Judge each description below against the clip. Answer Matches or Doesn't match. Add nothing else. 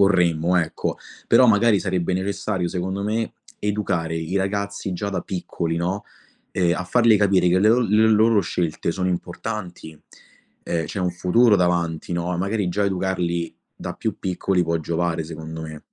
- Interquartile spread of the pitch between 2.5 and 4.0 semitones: Matches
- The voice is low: Matches